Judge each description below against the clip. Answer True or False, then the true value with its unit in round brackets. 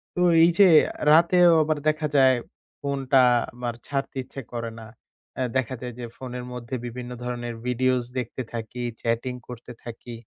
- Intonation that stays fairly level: True (2.1 semitones)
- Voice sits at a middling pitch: False (125 Hz)